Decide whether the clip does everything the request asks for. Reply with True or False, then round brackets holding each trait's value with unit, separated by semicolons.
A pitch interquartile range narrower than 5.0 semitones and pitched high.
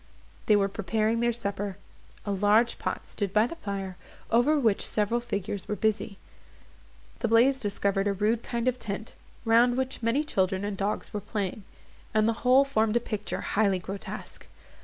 True (2.8 semitones; 215 Hz)